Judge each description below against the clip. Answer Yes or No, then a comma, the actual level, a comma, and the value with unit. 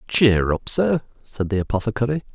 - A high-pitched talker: No, low, 115 Hz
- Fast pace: No, average, 155 wpm